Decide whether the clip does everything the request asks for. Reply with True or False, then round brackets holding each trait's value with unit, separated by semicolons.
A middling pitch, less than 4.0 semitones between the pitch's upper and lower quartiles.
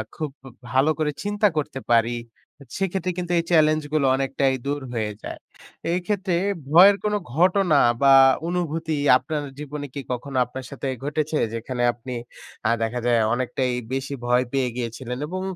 False (145 Hz; 4.8 semitones)